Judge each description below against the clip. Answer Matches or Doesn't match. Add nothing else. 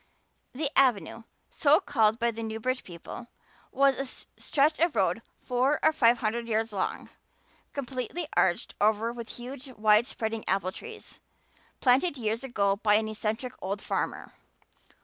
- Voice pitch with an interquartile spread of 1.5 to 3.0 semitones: Doesn't match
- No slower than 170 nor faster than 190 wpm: Doesn't match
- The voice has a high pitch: Matches